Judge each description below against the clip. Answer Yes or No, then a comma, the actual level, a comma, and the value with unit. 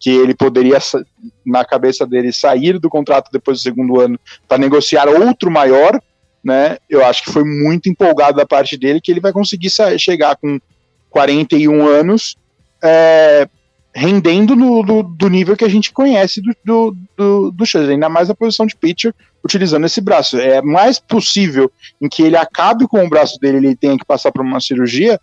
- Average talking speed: Yes, average, 190 wpm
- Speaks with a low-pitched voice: No, medium, 155 Hz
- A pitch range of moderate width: No, wide, 6.7 semitones